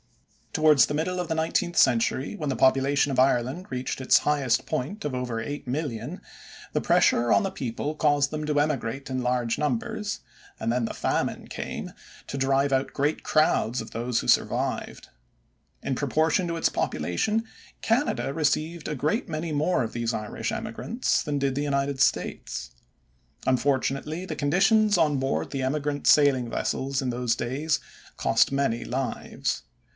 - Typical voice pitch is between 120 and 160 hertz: Yes, medium, 140 Hz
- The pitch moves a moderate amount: Yes, average, 3.5 semitones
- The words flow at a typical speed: Yes, average, 160 wpm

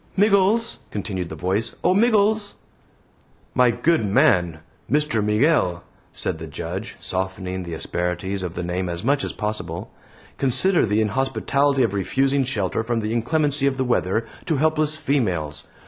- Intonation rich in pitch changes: Yes, wide, 7.8 semitones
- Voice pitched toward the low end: Yes, low, 115 Hz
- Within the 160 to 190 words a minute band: No, average, 145 wpm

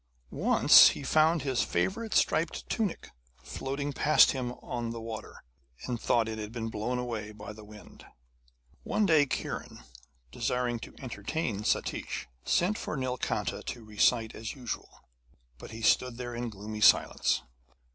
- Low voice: Yes, low, 120 Hz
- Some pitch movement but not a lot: Yes, average, 3.9 semitones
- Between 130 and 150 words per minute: Yes, average, 145 wpm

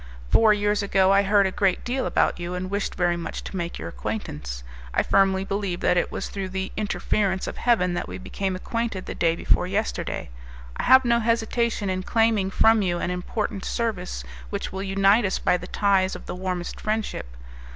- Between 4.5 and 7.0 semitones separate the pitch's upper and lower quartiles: No, average, 2.8 semitones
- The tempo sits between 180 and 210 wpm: Yes, average, 200 wpm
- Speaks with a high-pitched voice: Yes, high, 195 Hz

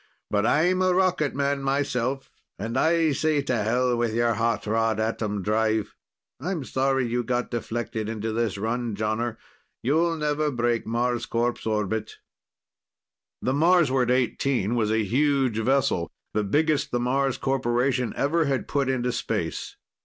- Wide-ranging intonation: No, average, 3.6 semitones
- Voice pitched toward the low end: Yes, low, 125 Hz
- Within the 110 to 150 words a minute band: Yes, average, 145 wpm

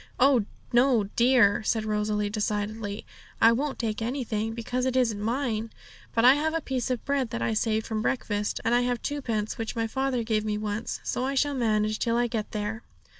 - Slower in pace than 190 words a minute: No, average, 200 wpm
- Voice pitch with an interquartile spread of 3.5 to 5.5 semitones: No, average, 3.0 semitones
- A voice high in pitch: Yes, high, 230 Hz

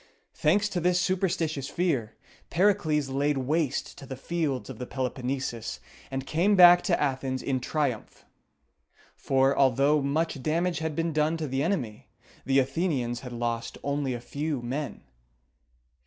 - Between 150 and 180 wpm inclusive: No, average, 140 wpm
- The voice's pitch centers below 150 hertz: Yes, medium, 140 Hz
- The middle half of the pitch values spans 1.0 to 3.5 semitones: No, average, 3.9 semitones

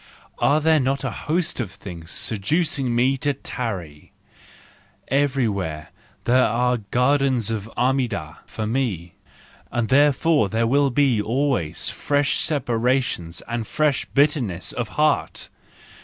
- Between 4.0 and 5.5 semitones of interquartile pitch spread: Yes, average, 4.5 semitones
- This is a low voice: Yes, low, 125 Hz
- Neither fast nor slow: No, slow, 120 wpm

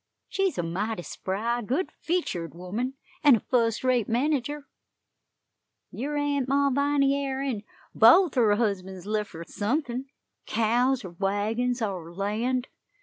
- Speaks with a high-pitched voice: Yes, high, 240 Hz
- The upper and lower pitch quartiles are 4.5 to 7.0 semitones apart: Yes, average, 5.1 semitones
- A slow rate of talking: Yes, slow, 130 wpm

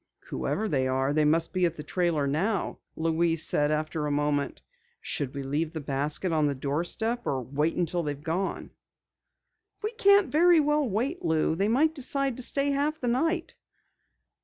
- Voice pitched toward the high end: No, medium, 165 Hz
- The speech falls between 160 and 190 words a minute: Yes, average, 175 wpm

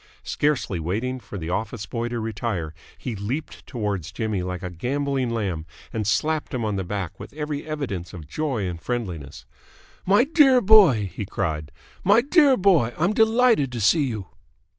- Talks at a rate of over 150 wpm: Yes, average, 170 wpm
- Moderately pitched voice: No, low, 115 Hz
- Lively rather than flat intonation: Yes, wide, 8.2 semitones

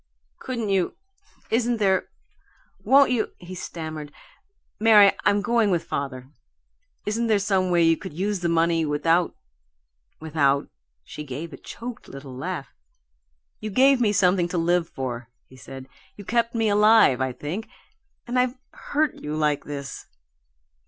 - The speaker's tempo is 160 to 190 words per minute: No, average, 150 wpm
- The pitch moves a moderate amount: No, wide, 6.6 semitones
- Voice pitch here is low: No, medium, 180 Hz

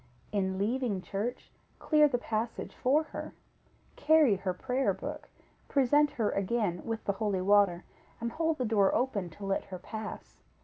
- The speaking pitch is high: Yes, high, 220 Hz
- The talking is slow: No, average, 160 wpm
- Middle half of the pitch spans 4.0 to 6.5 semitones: Yes, average, 4.8 semitones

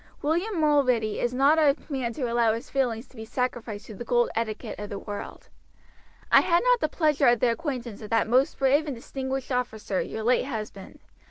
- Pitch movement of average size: Yes, average, 4.0 semitones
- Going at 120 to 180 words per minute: No, average, 200 wpm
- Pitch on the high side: Yes, very high, 250 Hz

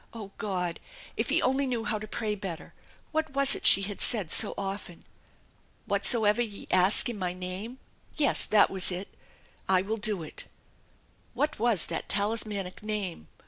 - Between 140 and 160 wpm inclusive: No, average, 180 wpm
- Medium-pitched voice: No, high, 205 Hz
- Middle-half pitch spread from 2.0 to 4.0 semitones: Yes, average, 3.4 semitones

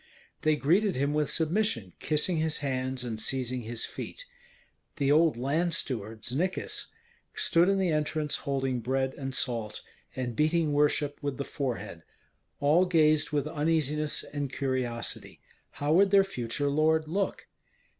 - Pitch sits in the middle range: Yes, medium, 145 Hz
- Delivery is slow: No, average, 145 wpm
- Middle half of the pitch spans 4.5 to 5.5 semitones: No, average, 3.6 semitones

